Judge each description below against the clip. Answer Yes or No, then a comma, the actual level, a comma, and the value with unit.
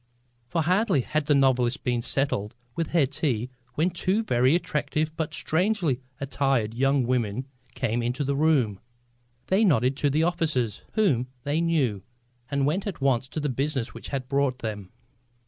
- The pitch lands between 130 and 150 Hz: Yes, medium, 140 Hz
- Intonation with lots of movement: No, average, 4.2 semitones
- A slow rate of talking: No, average, 165 wpm